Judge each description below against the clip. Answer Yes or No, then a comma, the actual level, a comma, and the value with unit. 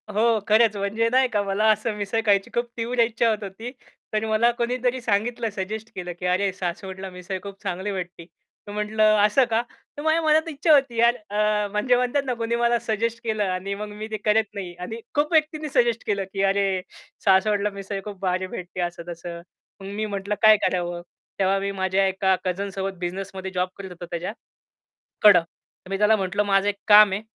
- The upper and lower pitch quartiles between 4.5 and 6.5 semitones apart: No, average, 3.0 semitones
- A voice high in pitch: Yes, high, 205 Hz